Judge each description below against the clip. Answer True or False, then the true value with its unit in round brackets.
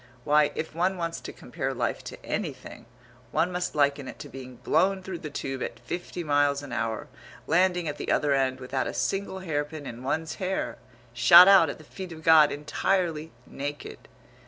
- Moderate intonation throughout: True (3.9 semitones)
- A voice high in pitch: False (155 Hz)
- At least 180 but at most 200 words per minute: True (185 wpm)